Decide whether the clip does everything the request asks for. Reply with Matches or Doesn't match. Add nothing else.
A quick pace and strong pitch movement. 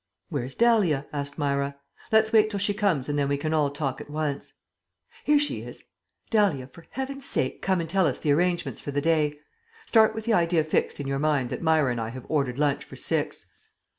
Matches